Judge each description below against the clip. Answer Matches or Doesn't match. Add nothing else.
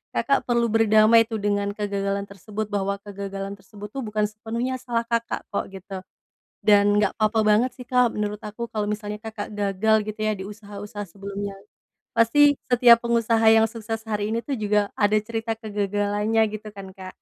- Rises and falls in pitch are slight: Matches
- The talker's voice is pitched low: Doesn't match